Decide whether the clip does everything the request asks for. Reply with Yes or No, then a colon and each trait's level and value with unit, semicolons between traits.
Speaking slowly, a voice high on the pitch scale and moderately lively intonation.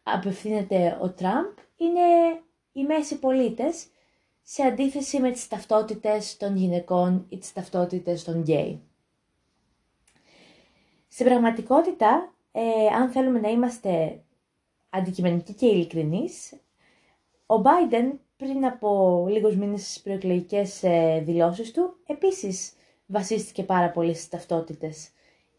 No: slow, 105 wpm; high, 210 Hz; wide, 6.2 semitones